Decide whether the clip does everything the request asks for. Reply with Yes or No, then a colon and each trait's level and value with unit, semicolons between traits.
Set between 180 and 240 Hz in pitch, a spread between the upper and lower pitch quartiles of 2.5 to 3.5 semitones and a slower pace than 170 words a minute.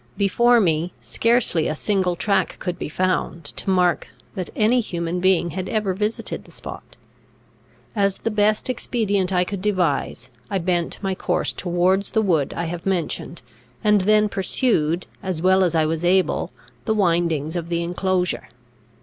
Yes: medium, 185 Hz; average, 2.9 semitones; average, 160 wpm